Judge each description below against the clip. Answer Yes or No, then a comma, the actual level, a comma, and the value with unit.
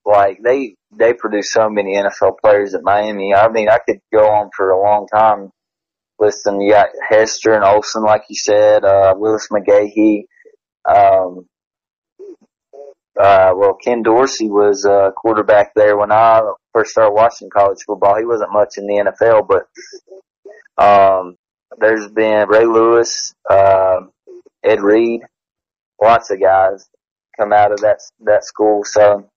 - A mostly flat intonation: Yes, narrow, 2.1 semitones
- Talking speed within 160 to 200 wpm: No, average, 150 wpm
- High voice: No, low, 105 Hz